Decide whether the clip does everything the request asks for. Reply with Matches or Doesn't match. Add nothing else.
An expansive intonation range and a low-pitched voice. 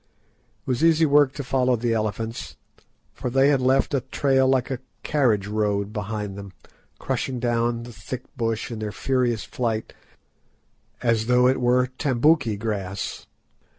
Doesn't match